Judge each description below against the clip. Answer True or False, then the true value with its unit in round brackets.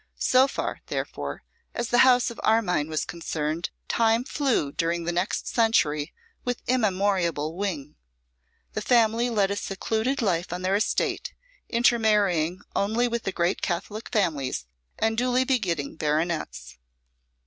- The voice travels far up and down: True (5.7 semitones)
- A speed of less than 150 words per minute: True (135 wpm)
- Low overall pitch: False (200 Hz)